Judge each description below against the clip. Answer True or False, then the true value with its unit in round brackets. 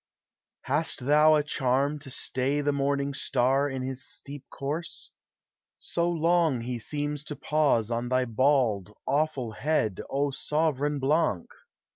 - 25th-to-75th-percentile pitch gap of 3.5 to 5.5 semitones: False (2.7 semitones)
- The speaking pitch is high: False (140 Hz)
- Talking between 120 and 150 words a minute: True (135 wpm)